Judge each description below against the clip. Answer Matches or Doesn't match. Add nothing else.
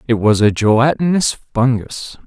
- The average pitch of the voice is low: Matches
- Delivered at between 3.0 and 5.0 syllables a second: Matches